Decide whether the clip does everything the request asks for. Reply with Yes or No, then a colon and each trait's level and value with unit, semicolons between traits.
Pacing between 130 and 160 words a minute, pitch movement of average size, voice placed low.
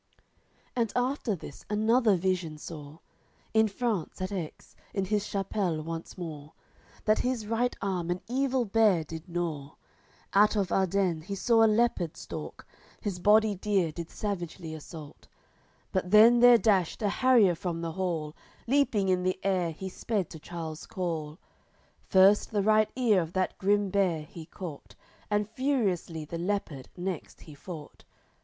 No: average, 155 wpm; average, 4.3 semitones; high, 190 Hz